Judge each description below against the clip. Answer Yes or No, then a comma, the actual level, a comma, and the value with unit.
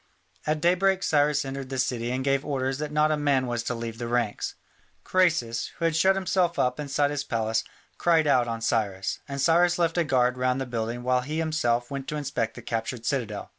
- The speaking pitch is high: No, low, 135 Hz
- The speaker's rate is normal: No, fast, 210 wpm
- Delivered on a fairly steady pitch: No, average, 4.2 semitones